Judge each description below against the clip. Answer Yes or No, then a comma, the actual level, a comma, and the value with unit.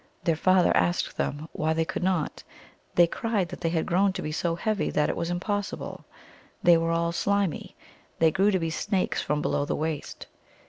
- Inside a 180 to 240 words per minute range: Yes, average, 195 wpm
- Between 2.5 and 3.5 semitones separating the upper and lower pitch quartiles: Yes, average, 2.9 semitones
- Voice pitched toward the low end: No, medium, 170 Hz